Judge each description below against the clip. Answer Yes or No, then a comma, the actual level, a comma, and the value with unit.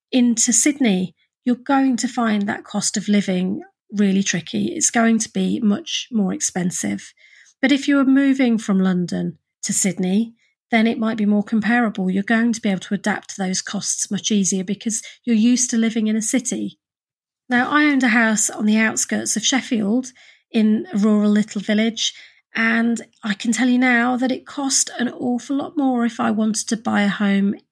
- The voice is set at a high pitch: Yes, high, 225 Hz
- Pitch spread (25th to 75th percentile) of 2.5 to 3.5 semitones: Yes, average, 3.2 semitones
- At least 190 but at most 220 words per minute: Yes, average, 195 wpm